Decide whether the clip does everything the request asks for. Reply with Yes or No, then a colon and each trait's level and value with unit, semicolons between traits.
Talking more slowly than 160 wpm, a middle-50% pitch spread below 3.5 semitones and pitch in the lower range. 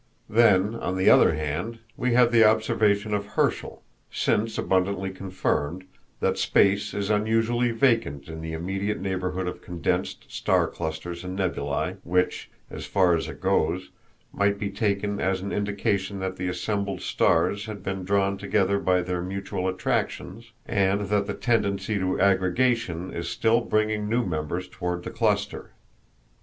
Yes: average, 150 wpm; narrow, 2.4 semitones; low, 100 Hz